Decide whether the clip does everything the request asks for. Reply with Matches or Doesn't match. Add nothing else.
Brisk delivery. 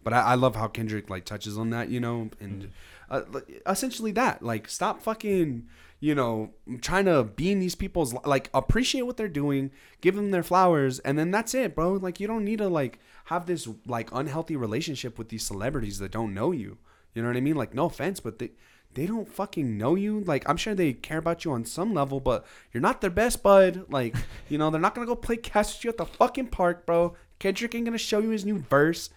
Matches